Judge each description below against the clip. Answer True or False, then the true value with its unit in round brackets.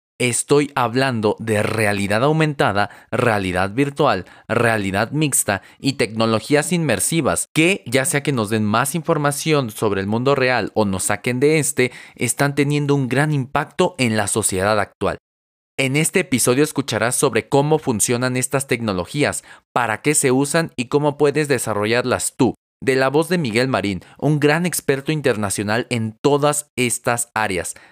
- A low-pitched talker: True (125 Hz)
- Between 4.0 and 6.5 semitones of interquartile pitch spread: True (5.0 semitones)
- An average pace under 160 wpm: True (150 wpm)